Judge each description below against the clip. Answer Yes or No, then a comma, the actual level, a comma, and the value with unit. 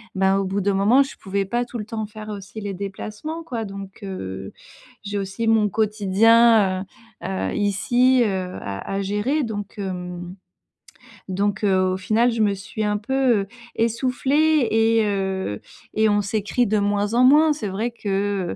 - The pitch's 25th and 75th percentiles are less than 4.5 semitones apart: Yes, average, 2.8 semitones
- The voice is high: Yes, high, 205 Hz